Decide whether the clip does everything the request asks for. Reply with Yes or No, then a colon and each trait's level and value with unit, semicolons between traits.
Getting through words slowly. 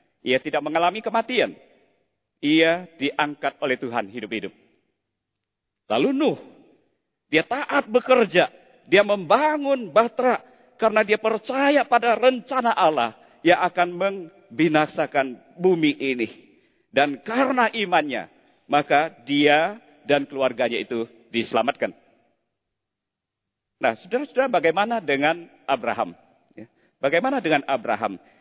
No: average, 95 wpm